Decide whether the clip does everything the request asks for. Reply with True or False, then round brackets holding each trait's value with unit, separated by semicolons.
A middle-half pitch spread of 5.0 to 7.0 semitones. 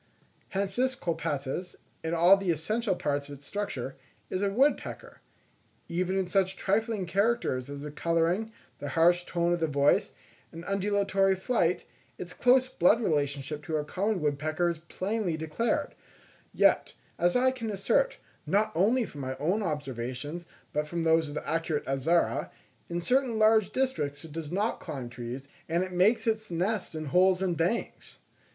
True (5.3 semitones)